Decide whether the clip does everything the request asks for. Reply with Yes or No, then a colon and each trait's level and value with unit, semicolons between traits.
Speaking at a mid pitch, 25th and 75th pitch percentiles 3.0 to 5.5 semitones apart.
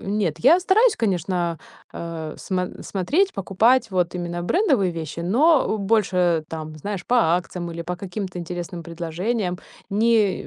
Yes: medium, 180 Hz; average, 4.3 semitones